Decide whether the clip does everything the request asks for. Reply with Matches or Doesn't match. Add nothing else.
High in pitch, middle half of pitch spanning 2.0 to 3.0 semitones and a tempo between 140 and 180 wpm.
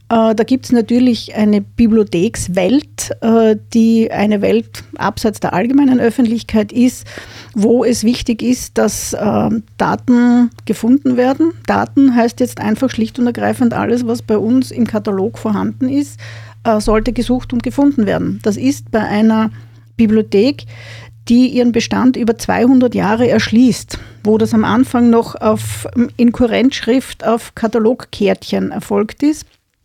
Doesn't match